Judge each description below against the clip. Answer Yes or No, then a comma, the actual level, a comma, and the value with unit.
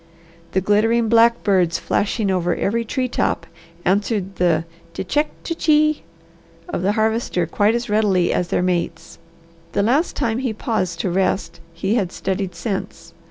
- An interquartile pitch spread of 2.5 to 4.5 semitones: Yes, average, 4.2 semitones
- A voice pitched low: No, high, 205 Hz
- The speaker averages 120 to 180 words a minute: Yes, average, 150 wpm